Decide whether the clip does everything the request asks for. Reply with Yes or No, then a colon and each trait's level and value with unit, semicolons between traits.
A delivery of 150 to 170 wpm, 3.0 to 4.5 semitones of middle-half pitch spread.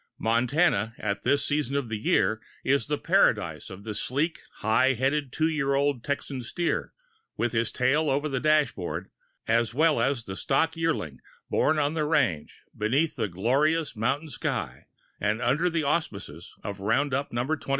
No: average, 165 wpm; average, 5.1 semitones